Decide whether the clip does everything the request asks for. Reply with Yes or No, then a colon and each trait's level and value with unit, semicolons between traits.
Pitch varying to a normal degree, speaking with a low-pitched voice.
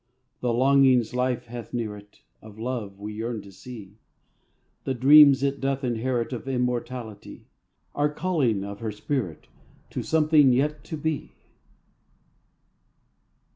Yes: average, 3.8 semitones; low, 125 Hz